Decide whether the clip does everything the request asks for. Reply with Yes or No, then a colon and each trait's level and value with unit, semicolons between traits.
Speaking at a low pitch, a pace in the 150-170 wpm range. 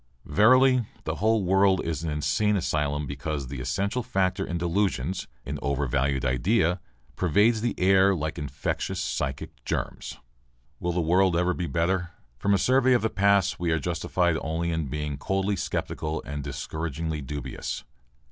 Yes: very low, 85 Hz; average, 155 wpm